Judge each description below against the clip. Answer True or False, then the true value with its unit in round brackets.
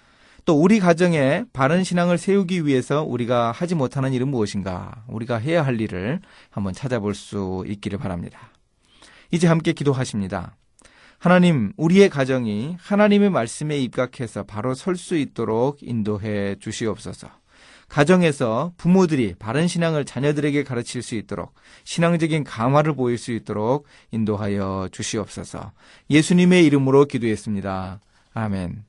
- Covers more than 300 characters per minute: True (330 characters per minute)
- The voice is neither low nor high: False (125 Hz)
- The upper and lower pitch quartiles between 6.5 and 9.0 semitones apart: True (7.6 semitones)